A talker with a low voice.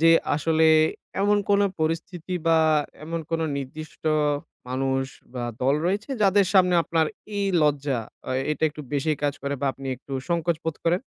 No: medium, 160 Hz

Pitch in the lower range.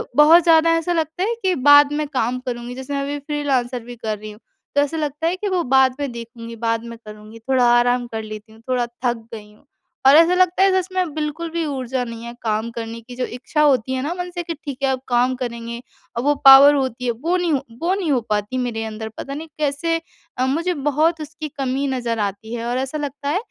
No: very high, 265 Hz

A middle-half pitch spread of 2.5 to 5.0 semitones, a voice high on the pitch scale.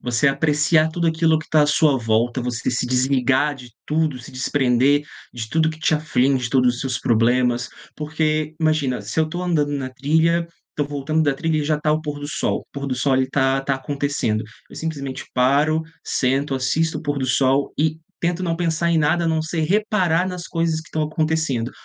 No: average, 3.4 semitones; medium, 145 Hz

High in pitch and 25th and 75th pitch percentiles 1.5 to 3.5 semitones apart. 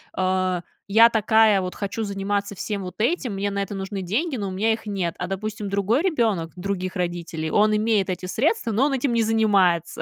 Yes: high, 200 Hz; average, 3.0 semitones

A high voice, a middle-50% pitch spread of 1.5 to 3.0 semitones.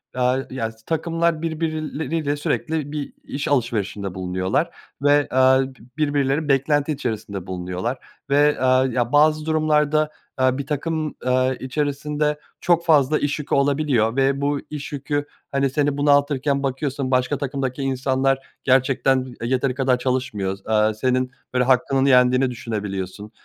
No: low, 135 Hz; narrow, 2.6 semitones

